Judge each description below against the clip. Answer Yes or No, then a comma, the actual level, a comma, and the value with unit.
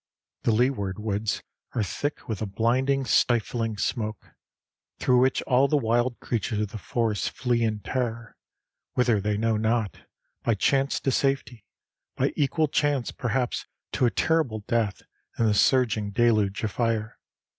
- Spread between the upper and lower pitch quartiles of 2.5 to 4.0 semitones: Yes, average, 3.0 semitones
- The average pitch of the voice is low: Yes, low, 115 Hz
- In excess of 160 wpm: No, average, 150 wpm